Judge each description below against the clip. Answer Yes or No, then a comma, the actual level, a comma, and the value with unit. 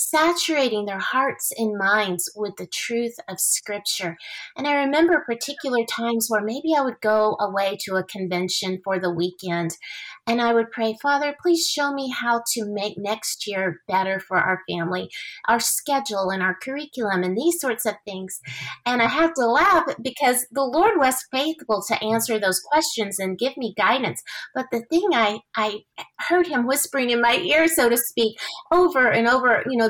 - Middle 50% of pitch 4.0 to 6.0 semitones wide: Yes, wide, 5.4 semitones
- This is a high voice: Yes, high, 230 Hz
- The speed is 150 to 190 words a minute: Yes, average, 185 wpm